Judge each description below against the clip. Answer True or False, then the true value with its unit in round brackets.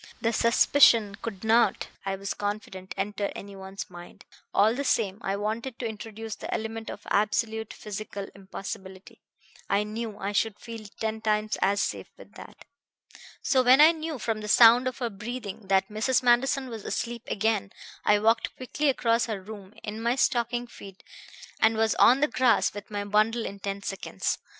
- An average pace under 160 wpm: False (175 wpm)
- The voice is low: False (220 Hz)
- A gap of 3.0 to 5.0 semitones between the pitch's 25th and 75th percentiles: False (2.6 semitones)